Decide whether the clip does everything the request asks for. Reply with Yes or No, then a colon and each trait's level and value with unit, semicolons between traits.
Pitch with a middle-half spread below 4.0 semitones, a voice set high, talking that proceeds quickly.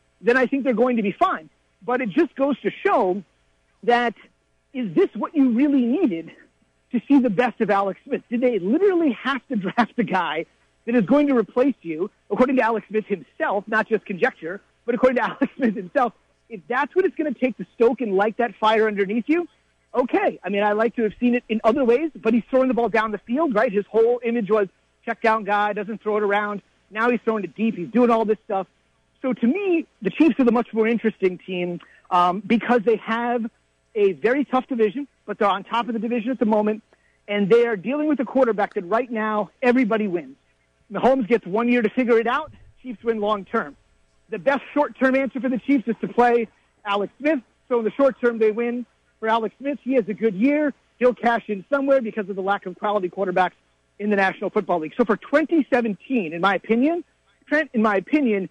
Yes: average, 3.6 semitones; high, 230 Hz; fast, 225 wpm